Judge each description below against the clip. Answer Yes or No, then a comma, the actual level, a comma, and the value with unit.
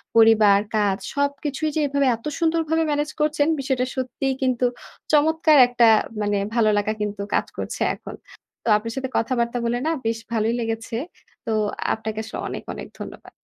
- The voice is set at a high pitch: Yes, high, 245 Hz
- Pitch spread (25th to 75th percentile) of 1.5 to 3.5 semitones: No, average, 4.3 semitones